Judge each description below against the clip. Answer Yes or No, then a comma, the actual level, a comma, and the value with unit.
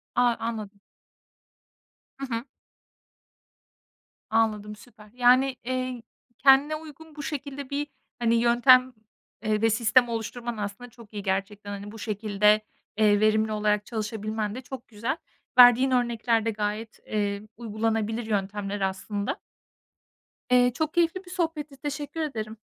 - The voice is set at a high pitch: Yes, high, 225 Hz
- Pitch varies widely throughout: No, average, 3.4 semitones